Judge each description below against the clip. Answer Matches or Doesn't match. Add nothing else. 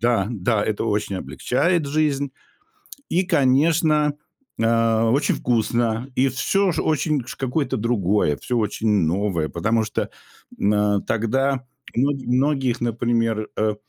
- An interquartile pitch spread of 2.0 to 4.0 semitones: Doesn't match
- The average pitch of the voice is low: Matches